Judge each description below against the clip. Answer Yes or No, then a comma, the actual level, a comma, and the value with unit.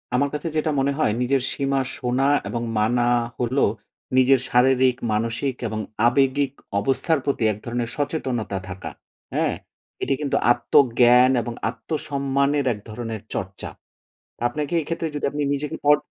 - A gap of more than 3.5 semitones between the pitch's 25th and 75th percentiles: No, average, 2.9 semitones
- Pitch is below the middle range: Yes, low, 130 Hz